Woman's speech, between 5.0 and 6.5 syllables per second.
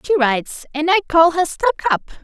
Yes: female; 5.6 syllables/s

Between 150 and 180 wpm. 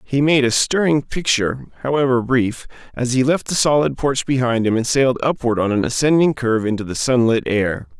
No: average, 195 wpm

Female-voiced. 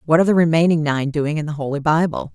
Yes: female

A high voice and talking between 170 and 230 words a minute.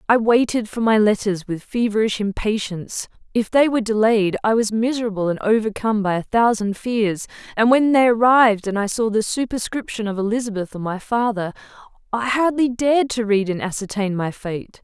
Yes: high, 220 Hz; average, 180 wpm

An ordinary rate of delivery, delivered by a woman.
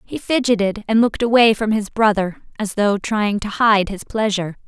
Yes: average, 195 wpm; female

